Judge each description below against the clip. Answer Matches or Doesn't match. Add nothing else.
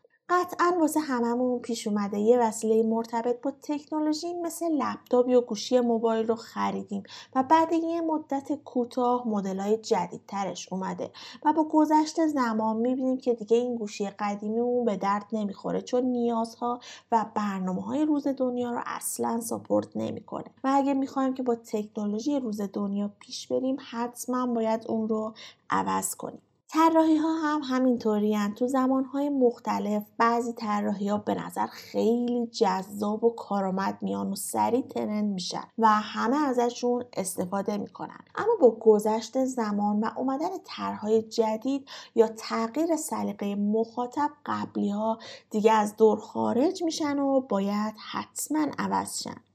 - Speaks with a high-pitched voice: Matches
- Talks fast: Doesn't match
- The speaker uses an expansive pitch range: Doesn't match